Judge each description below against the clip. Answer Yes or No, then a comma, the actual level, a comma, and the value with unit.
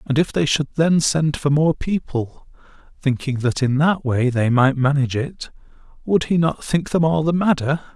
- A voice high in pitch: No, medium, 145 Hz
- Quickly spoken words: No, average, 195 wpm